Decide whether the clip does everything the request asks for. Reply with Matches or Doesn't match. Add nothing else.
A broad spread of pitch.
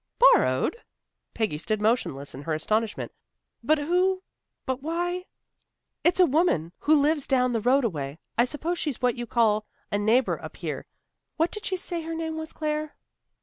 Matches